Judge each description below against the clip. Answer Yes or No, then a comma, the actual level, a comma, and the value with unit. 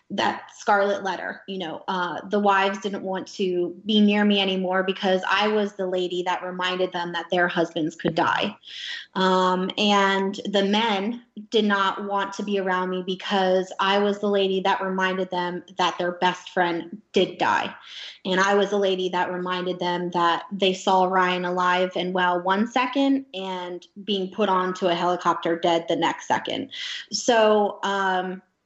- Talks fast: No, average, 170 wpm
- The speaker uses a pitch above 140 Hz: Yes, high, 190 Hz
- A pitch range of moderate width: No, narrow, 1.8 semitones